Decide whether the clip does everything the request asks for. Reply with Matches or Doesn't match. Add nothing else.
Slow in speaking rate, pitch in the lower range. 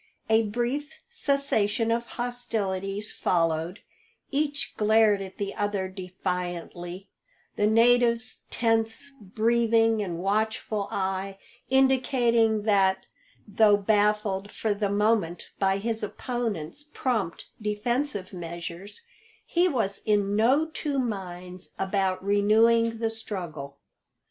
Doesn't match